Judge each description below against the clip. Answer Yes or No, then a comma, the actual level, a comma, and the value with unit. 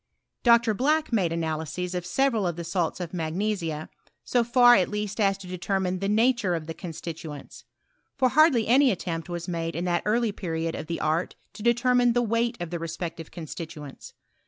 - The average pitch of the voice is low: No, medium, 185 Hz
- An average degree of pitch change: No, wide, 5.9 semitones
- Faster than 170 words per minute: Yes, average, 190 wpm